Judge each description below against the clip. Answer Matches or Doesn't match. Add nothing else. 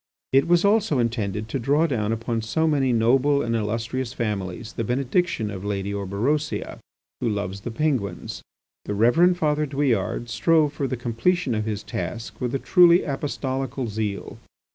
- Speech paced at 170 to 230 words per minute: Doesn't match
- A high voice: Doesn't match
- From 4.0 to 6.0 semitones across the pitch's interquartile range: Matches